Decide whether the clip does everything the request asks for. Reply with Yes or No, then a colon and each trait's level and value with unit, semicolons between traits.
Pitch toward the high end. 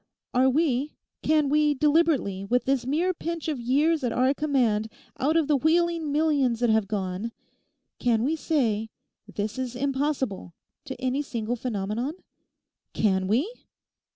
Yes: very high, 265 Hz